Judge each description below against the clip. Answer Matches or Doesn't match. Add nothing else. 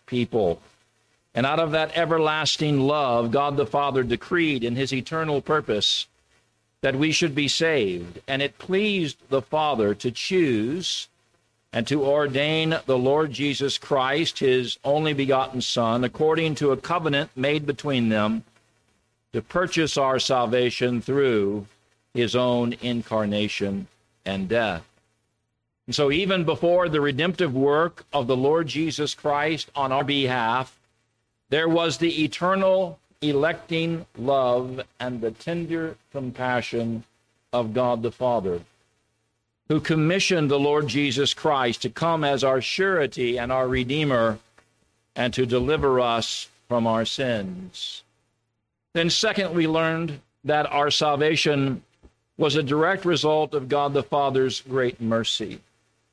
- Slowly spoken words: Matches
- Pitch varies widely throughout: Doesn't match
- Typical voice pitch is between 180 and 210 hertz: Doesn't match